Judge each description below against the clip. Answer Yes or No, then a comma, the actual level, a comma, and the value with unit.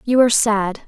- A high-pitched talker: Yes, high, 220 Hz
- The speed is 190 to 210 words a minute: Yes, fast, 205 wpm